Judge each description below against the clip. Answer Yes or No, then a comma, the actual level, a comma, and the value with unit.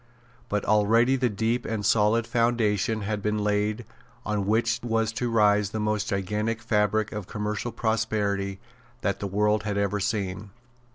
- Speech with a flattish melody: Yes, narrow, 1.6 semitones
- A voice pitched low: Yes, low, 105 Hz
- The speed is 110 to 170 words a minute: Yes, average, 155 wpm